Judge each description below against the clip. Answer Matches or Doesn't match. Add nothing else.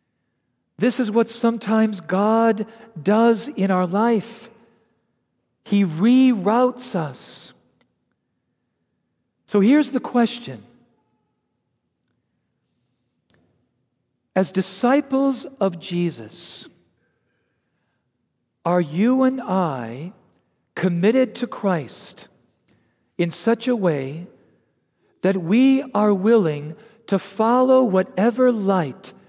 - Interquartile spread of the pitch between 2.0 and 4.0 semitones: Doesn't match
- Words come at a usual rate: Doesn't match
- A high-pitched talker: Matches